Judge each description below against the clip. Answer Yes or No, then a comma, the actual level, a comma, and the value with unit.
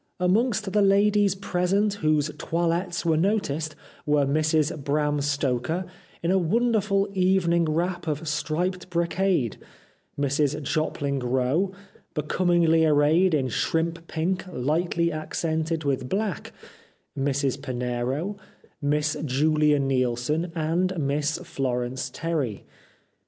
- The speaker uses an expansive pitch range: No, average, 4.0 semitones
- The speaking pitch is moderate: Yes, medium, 160 Hz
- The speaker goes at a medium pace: No, slow, 110 wpm